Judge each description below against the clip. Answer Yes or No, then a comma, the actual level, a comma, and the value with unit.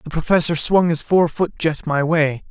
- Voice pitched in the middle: Yes, medium, 160 Hz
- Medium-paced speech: No, fast, 215 wpm